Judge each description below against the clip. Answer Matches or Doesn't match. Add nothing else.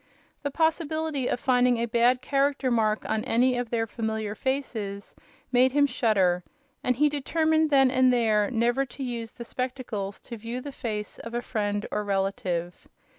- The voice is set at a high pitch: Matches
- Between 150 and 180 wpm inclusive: Matches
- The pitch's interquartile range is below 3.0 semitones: Doesn't match